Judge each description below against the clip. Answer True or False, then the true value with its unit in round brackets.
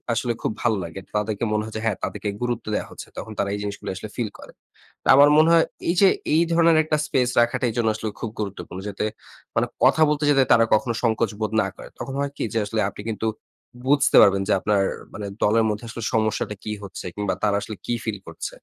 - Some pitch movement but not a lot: True (3.2 semitones)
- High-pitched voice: False (110 Hz)